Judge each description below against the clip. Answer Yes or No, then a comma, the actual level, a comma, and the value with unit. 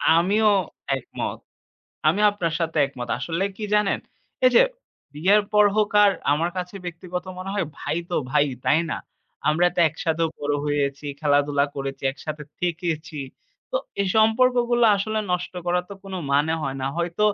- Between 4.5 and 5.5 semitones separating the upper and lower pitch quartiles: Yes, average, 5.1 semitones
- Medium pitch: Yes, medium, 170 Hz